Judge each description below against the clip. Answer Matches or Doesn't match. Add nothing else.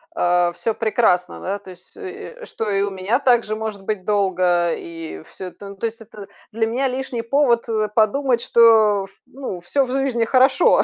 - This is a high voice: Matches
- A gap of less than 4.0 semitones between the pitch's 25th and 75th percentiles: Doesn't match